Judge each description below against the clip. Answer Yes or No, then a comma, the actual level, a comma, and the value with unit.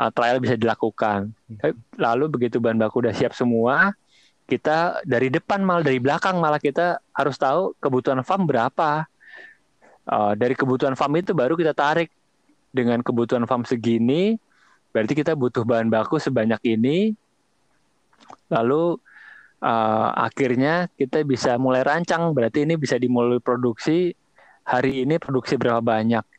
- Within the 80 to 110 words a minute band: No, average, 130 wpm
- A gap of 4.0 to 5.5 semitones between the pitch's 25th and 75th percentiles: Yes, average, 4.9 semitones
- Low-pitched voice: Yes, low, 130 Hz